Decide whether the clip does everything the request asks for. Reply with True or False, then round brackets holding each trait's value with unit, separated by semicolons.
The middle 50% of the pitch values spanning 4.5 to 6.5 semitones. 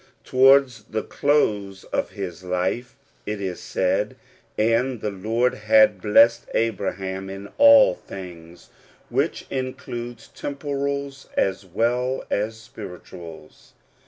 True (4.8 semitones)